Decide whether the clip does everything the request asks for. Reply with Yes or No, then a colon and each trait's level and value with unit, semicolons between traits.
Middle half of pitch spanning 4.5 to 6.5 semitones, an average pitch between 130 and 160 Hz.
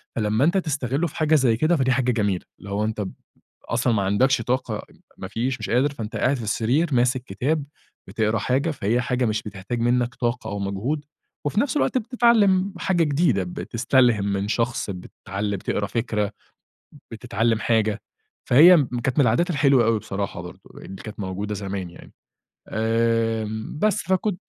No: average, 4.9 semitones; low, 120 Hz